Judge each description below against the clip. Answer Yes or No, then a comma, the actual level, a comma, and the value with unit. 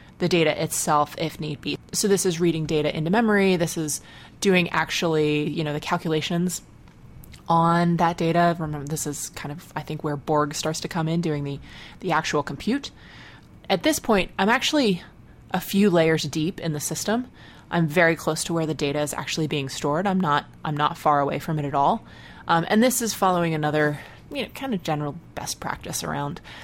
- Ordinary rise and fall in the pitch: Yes, average, 3.1 semitones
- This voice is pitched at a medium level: Yes, medium, 160 Hz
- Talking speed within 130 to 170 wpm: No, average, 200 wpm